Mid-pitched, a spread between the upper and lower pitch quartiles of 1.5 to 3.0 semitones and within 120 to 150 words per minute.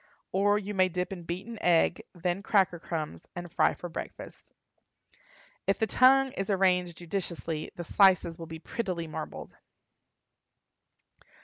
Yes: medium, 180 Hz; narrow, 2.6 semitones; slow, 135 wpm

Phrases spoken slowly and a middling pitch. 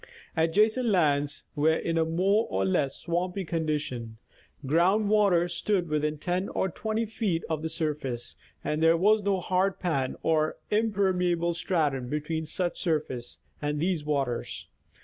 No: average, 145 wpm; medium, 165 Hz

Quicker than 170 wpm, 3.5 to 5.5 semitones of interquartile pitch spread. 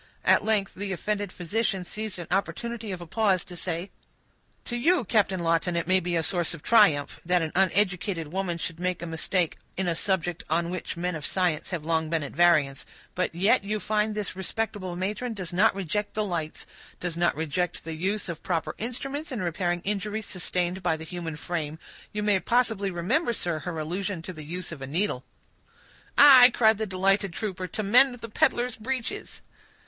Yes: average, 190 wpm; average, 3.8 semitones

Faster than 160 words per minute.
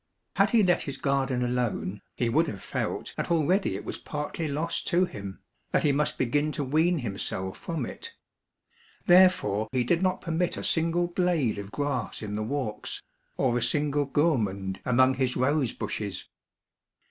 Yes: average, 170 wpm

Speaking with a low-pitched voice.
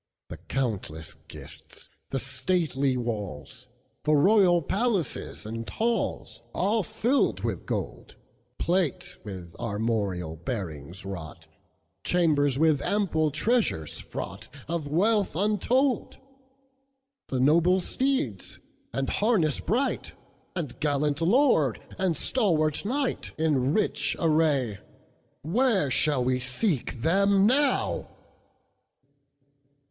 No: medium, 155 Hz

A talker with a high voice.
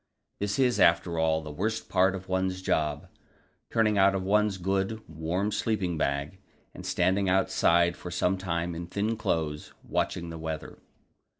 No: very low, 90 Hz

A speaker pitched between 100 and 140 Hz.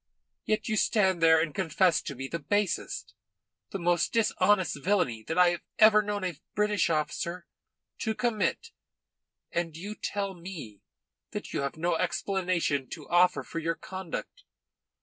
No: medium, 180 Hz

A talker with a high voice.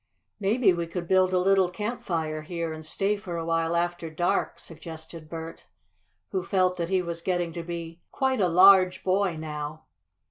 No: medium, 175 Hz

